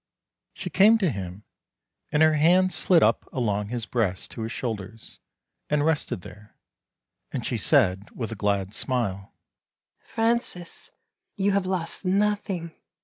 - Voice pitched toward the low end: Yes, low, 130 Hz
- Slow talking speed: No, average, 145 wpm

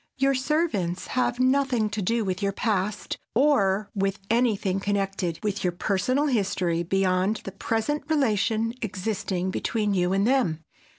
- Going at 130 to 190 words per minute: Yes, average, 140 wpm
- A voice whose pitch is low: No, high, 205 Hz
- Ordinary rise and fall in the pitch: Yes, average, 4.2 semitones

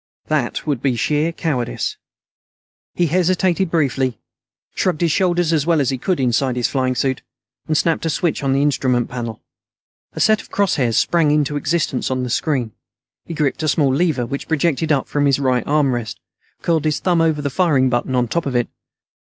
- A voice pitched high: No, medium, 145 Hz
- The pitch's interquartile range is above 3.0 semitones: Yes, average, 4.2 semitones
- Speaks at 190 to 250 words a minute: Yes, average, 195 wpm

